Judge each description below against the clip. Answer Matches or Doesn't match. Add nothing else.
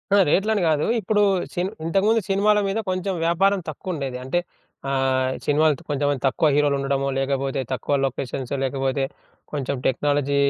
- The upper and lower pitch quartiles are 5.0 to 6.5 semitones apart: Matches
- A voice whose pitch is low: Doesn't match